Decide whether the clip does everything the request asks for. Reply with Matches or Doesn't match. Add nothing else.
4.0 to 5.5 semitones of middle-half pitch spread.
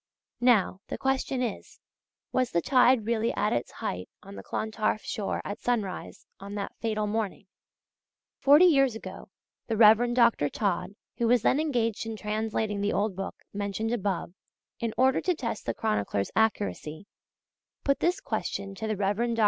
Doesn't match